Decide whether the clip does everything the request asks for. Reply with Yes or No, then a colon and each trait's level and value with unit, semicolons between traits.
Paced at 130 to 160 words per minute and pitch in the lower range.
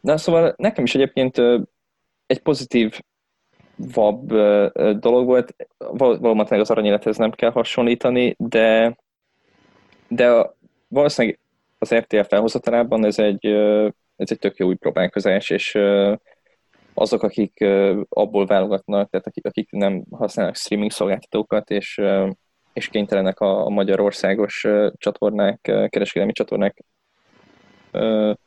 No: slow, 105 wpm; low, 105 Hz